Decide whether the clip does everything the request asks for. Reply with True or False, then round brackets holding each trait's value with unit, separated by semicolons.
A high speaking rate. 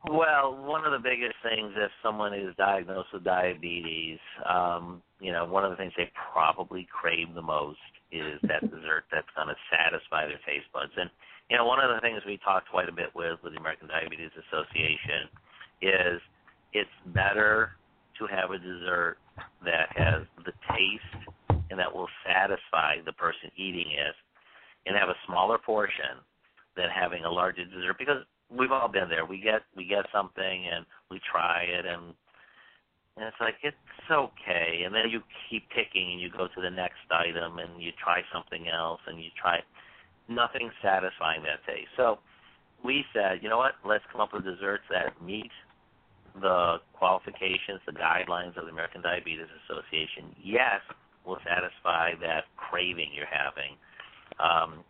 False (170 wpm)